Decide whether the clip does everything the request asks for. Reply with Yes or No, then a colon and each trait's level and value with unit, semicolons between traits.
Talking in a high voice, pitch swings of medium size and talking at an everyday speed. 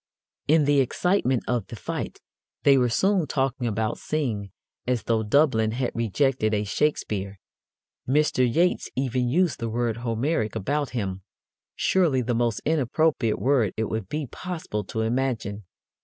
No: low, 125 Hz; average, 4.6 semitones; average, 145 wpm